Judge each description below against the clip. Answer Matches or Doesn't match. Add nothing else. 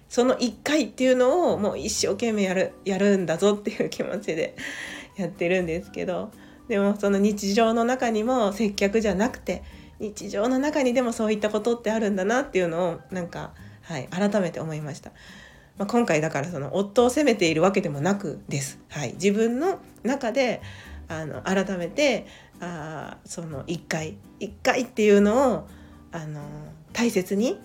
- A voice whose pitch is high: Matches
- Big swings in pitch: Matches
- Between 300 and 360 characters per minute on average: Matches